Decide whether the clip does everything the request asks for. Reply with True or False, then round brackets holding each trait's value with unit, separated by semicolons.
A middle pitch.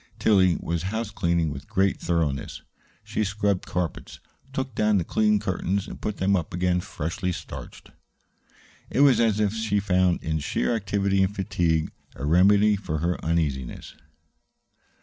False (95 Hz)